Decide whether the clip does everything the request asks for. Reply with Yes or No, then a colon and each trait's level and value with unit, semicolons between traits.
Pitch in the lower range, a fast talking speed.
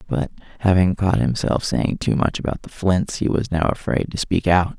Yes: very low, 95 Hz; fast, 215 wpm